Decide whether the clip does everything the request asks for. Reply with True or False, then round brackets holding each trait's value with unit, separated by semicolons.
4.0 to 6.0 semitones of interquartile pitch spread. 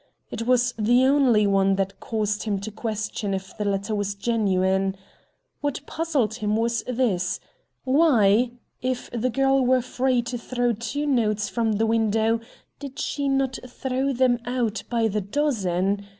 False (3.6 semitones)